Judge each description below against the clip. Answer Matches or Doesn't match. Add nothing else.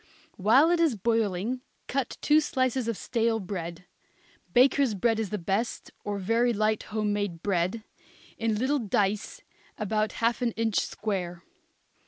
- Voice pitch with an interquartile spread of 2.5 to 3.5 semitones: Matches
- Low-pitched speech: Doesn't match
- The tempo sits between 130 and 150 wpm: Matches